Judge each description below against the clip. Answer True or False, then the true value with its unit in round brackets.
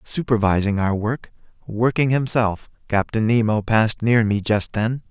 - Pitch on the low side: True (110 Hz)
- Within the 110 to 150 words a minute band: True (140 wpm)